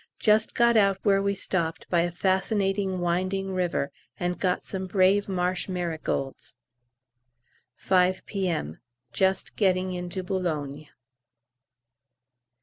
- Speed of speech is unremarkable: No, slow, 110 wpm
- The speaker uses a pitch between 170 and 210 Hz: Yes, medium, 185 Hz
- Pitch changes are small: Yes, narrow, 1.7 semitones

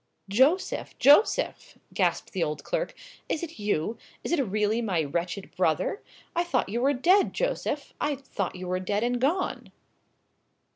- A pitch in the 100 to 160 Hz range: No, high, 240 Hz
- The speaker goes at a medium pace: Yes, average, 145 wpm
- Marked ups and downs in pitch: Yes, wide, 8.2 semitones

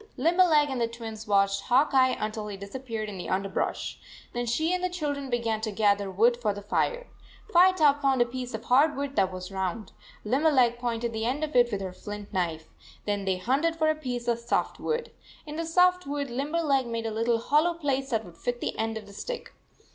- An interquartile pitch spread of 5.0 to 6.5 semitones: Yes, wide, 5.4 semitones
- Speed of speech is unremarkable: No, fast, 215 wpm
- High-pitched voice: Yes, high, 240 Hz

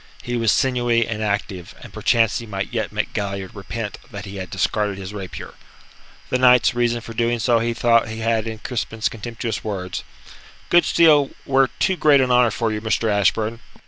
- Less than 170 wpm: No, average, 190 wpm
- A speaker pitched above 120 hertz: No, low, 115 Hz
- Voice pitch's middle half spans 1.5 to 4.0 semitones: Yes, average, 2.7 semitones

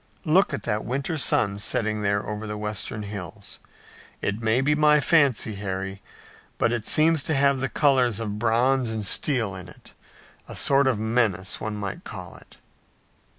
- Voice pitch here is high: No, low, 110 Hz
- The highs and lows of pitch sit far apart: No, average, 4.6 semitones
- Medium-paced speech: Yes, average, 170 wpm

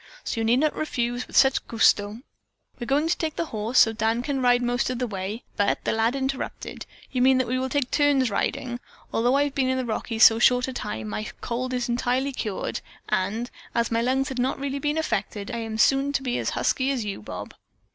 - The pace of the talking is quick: Yes, fast, 235 wpm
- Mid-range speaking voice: No, high, 245 Hz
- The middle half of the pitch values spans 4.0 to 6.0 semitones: No, average, 2.9 semitones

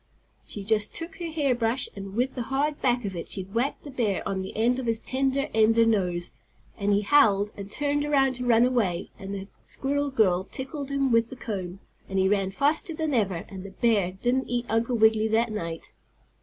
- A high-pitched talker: Yes, high, 225 Hz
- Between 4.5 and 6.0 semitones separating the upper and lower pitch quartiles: Yes, average, 5.2 semitones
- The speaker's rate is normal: No, fast, 210 wpm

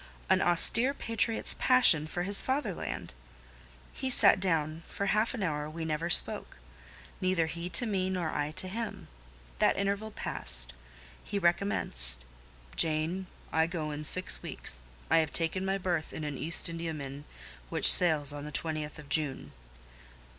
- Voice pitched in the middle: Yes, medium, 165 Hz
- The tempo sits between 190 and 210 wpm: No, average, 155 wpm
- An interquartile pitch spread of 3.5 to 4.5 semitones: Yes, average, 4.1 semitones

